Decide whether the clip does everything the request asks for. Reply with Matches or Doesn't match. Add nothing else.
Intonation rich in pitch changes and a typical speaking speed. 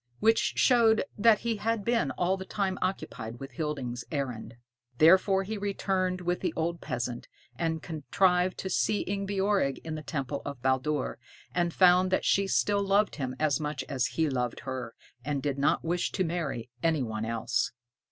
Matches